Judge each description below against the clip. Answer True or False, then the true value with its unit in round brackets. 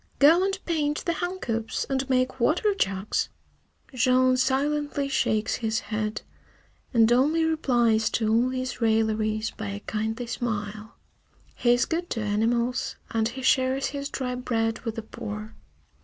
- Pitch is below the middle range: False (245 Hz)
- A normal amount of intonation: True (3.6 semitones)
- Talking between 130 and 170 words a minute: True (150 wpm)